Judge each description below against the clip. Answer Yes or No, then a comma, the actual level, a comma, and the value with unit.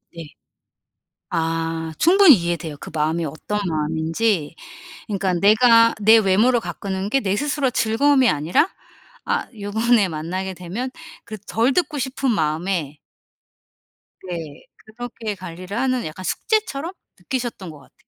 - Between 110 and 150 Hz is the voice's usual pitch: No, high, 200 Hz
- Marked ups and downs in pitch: Yes, wide, 6.7 semitones